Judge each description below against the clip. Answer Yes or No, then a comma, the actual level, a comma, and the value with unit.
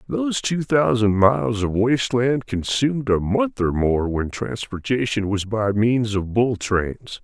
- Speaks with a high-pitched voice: No, low, 115 Hz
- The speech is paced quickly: No, average, 165 wpm